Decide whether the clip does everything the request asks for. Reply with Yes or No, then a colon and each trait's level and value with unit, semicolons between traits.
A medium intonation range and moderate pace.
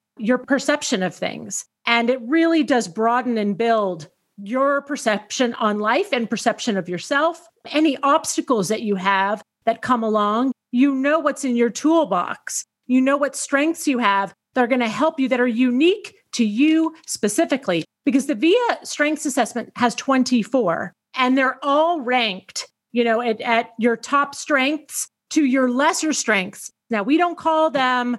Yes: average, 4.5 semitones; average, 165 wpm